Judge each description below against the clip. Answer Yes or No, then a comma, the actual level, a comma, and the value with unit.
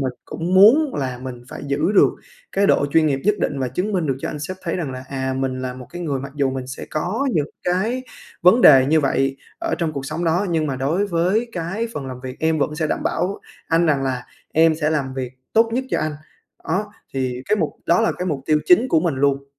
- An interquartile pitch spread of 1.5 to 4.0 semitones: No, average, 5.2 semitones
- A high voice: No, medium, 155 Hz